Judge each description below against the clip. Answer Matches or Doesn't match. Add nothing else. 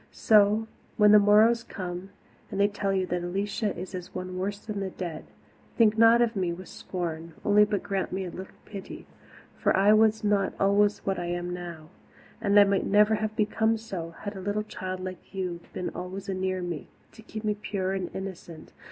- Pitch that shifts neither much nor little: Doesn't match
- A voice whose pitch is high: Matches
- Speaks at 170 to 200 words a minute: Matches